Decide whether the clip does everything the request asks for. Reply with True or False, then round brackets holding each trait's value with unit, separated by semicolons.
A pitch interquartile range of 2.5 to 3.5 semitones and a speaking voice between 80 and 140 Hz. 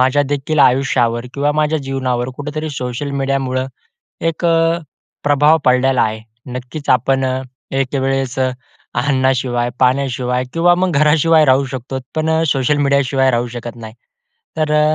True (2.8 semitones; 135 Hz)